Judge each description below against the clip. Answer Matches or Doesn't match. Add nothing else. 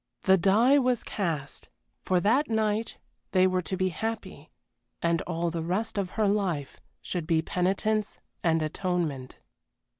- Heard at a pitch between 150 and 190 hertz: Matches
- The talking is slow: Doesn't match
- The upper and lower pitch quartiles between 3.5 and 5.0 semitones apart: Matches